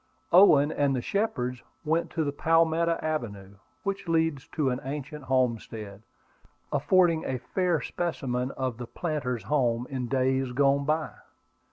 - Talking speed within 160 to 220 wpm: No, average, 140 wpm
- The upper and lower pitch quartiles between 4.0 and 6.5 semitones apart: Yes, average, 4.3 semitones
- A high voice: No, medium, 140 Hz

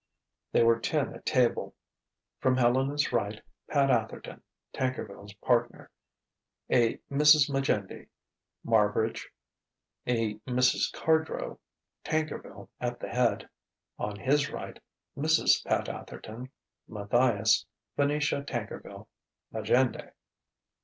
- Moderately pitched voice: No, low, 125 Hz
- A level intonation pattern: No, average, 4.0 semitones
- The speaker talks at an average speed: No, slow, 95 wpm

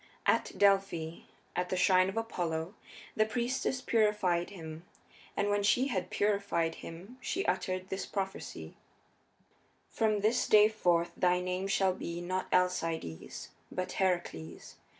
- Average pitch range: Yes, average, 3.1 semitones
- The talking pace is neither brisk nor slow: No, slow, 130 wpm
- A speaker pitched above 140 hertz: Yes, medium, 185 Hz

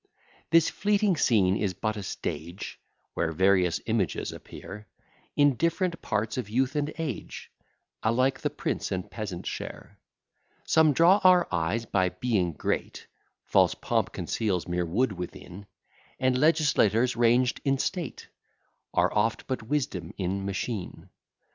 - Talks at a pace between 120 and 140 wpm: Yes, slow, 135 wpm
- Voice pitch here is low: Yes, low, 110 Hz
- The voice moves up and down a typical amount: No, wide, 6.6 semitones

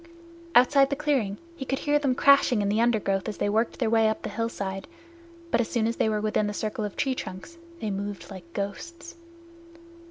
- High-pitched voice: Yes, high, 220 Hz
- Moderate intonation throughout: Yes, average, 4.7 semitones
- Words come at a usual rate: No, fast, 215 wpm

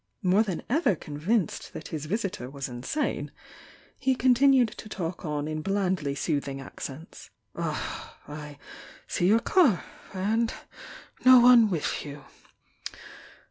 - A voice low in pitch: No, medium, 185 Hz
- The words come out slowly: Yes, slow, 130 wpm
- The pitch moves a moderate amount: No, wide, 7.6 semitones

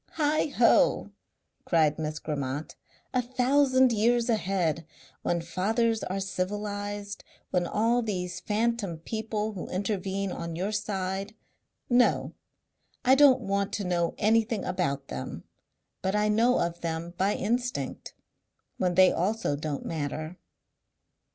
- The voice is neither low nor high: No, high, 200 Hz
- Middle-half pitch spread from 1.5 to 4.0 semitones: No, average, 4.7 semitones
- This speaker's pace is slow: Yes, slow, 120 wpm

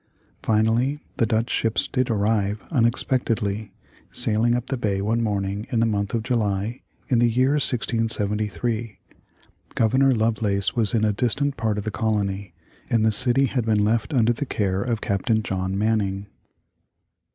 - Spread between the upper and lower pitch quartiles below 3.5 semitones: Yes, narrow, 2.6 semitones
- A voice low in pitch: Yes, low, 110 Hz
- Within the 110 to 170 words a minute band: Yes, average, 155 wpm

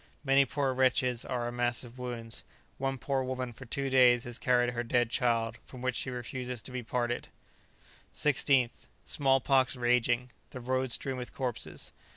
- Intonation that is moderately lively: No, narrow, 1.5 semitones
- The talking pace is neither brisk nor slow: Yes, average, 175 wpm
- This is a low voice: Yes, low, 125 Hz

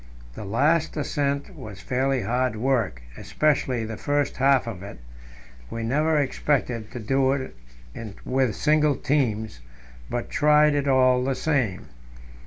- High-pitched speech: No, low, 130 Hz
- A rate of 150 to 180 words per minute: No, slow, 135 wpm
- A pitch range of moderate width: Yes, average, 3.9 semitones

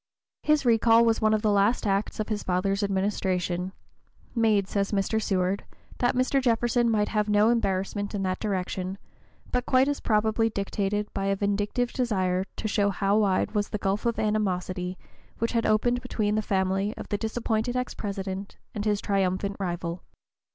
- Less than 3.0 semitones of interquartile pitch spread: Yes, narrow, 2.5 semitones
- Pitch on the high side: Yes, high, 205 Hz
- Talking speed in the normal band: Yes, average, 180 wpm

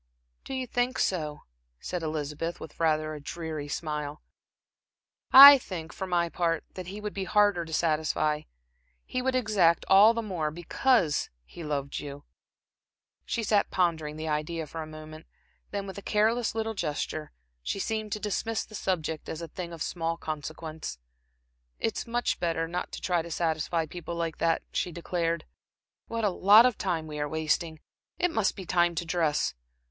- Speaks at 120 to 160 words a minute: No, average, 175 wpm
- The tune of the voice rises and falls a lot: No, average, 4.4 semitones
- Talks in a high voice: No, medium, 170 Hz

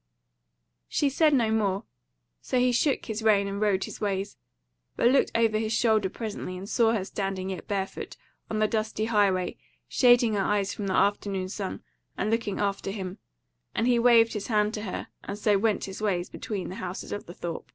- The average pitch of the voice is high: Yes, high, 210 Hz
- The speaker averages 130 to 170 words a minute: No, average, 195 wpm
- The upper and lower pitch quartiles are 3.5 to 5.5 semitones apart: No, narrow, 2.5 semitones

